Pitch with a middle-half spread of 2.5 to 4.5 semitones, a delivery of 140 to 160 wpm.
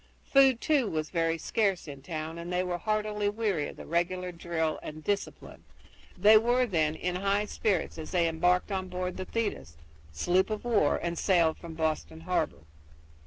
No: average, 4.2 semitones; average, 175 wpm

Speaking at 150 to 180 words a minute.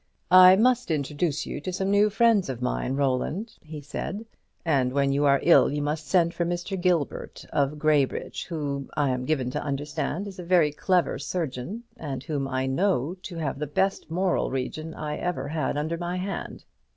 No: average, 190 wpm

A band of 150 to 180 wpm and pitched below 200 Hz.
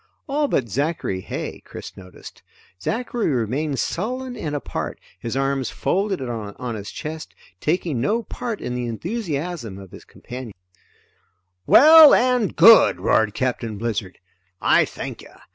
No: slow, 135 wpm; medium, 140 Hz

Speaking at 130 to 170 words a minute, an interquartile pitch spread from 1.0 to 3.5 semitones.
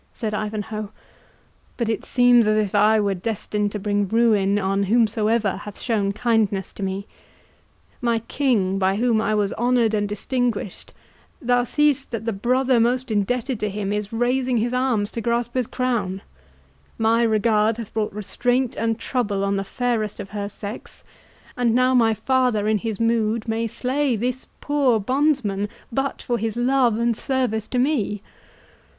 Yes: average, 160 wpm; average, 2.9 semitones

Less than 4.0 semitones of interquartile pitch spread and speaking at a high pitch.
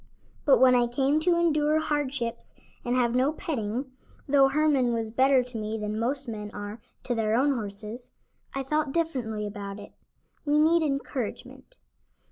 No: average, 4.7 semitones; very high, 255 Hz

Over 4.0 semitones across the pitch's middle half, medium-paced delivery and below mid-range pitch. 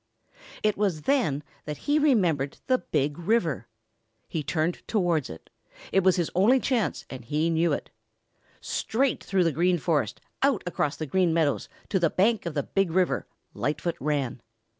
No: average, 5.0 semitones; average, 165 wpm; medium, 170 Hz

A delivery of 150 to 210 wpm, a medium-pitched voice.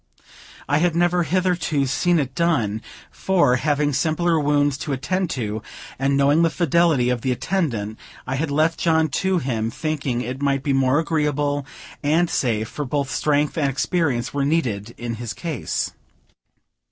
Yes: average, 160 wpm; medium, 145 Hz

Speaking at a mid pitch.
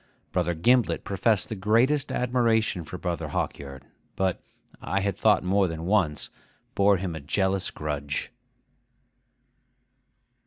No: very low, 95 Hz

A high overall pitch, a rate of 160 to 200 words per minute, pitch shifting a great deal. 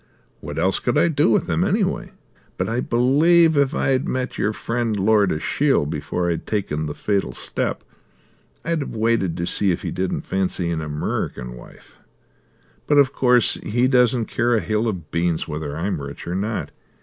No: low, 105 Hz; average, 180 wpm; wide, 6.5 semitones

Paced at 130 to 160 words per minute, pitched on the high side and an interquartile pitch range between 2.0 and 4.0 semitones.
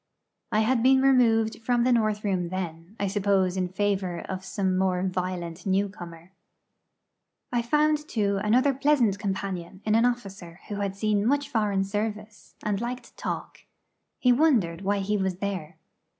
Yes: average, 155 wpm; high, 205 Hz; average, 3.6 semitones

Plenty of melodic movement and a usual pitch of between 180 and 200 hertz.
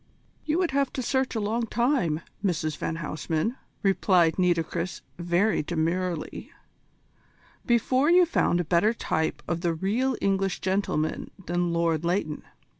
Yes: wide, 5.8 semitones; medium, 185 Hz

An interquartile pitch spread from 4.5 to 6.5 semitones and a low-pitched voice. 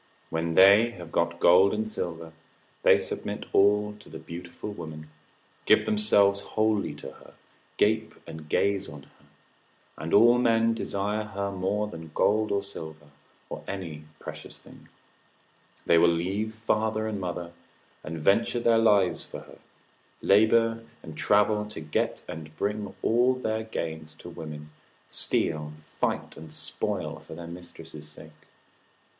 Yes: average, 4.8 semitones; low, 100 Hz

